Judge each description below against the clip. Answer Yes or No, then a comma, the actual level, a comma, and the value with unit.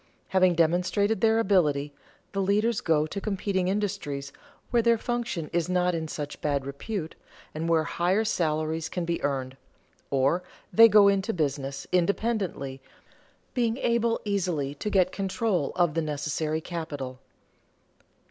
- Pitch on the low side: No, medium, 175 Hz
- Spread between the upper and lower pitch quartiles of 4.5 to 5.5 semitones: Yes, average, 5.0 semitones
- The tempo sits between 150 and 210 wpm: No, average, 140 wpm